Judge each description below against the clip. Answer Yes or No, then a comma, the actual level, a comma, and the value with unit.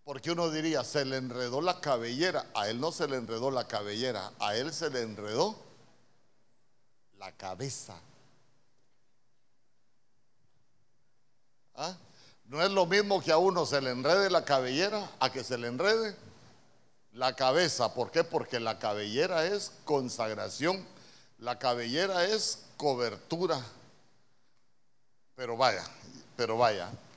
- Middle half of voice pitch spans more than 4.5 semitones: Yes, average, 5.0 semitones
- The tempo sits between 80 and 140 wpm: Yes, average, 130 wpm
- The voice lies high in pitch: No, low, 130 Hz